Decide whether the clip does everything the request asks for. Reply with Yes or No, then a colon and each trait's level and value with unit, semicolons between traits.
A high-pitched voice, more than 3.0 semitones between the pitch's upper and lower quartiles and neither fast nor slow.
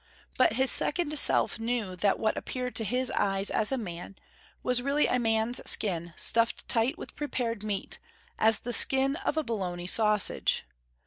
Yes: high, 230 Hz; average, 3.7 semitones; average, 170 wpm